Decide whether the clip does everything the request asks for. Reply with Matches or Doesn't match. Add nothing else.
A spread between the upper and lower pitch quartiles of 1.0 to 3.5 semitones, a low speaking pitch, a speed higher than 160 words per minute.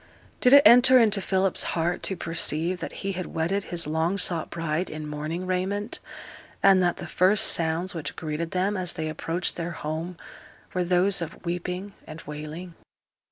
Doesn't match